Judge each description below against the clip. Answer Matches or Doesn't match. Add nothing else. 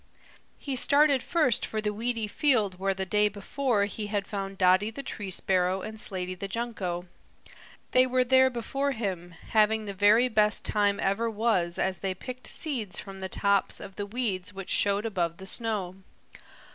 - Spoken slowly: Doesn't match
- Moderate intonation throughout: Matches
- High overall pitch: Matches